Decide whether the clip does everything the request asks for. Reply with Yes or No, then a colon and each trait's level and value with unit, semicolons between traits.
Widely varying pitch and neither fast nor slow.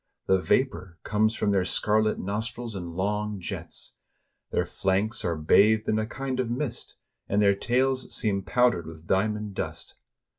No: average, 3.5 semitones; average, 160 wpm